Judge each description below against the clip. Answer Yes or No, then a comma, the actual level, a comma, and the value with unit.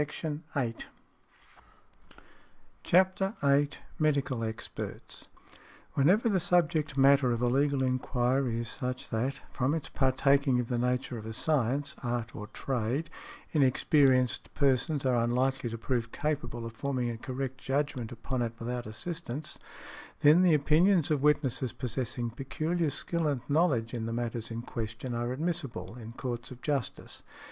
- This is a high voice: No, low, 130 Hz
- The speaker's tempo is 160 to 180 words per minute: No, average, 140 wpm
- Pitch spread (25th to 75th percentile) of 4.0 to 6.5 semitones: No, average, 3.6 semitones